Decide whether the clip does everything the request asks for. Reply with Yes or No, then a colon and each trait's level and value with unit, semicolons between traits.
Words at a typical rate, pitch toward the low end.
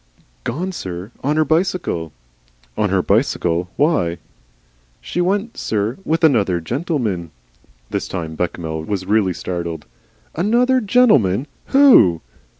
No: slow, 120 wpm; low, 110 Hz